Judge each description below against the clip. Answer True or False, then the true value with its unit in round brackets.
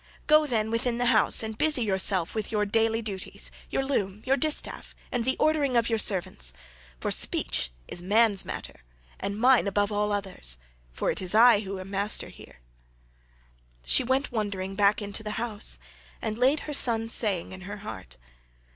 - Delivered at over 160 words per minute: True (175 wpm)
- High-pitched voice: True (215 Hz)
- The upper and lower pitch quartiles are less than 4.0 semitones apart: True (3.4 semitones)